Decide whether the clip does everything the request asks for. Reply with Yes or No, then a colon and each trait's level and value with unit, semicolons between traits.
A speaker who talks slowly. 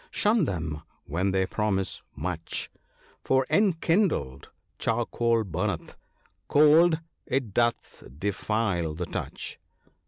Yes: slow, 105 wpm